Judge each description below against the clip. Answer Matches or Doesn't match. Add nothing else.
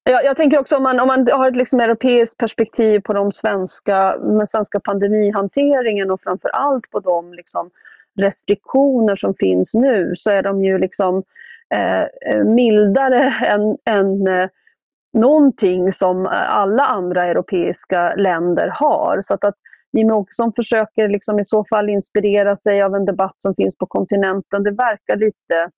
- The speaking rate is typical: Matches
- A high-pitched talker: Matches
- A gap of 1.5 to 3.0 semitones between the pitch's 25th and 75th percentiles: Doesn't match